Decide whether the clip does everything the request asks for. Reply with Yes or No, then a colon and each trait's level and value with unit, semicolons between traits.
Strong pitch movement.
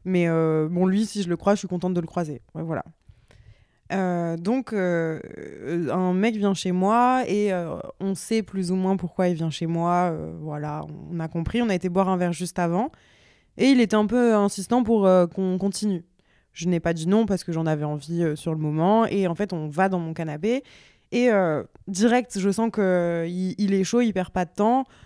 No: average, 3.4 semitones